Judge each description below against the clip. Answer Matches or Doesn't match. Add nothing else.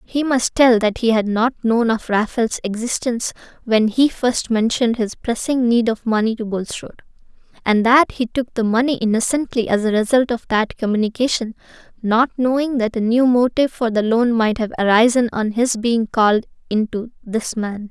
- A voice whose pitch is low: Doesn't match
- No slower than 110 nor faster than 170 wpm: Doesn't match